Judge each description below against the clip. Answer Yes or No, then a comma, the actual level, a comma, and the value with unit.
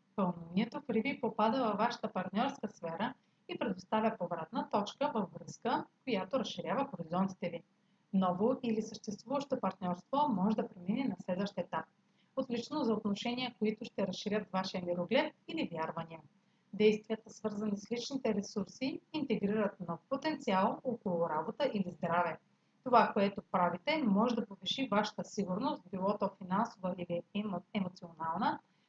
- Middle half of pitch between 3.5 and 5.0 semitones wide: Yes, average, 4.1 semitones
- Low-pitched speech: No, high, 210 Hz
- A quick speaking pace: No, average, 130 wpm